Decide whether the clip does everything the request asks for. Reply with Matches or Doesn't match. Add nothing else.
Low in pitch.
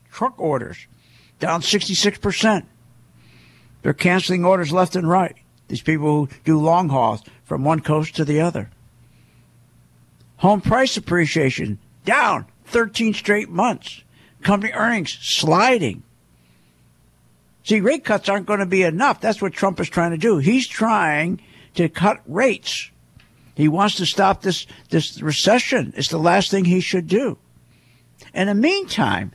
Doesn't match